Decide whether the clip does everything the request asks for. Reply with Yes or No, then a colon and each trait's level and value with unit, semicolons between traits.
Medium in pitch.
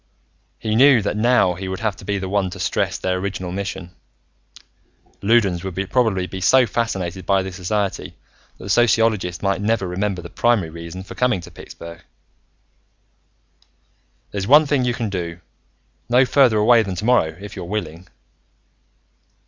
No: low, 100 Hz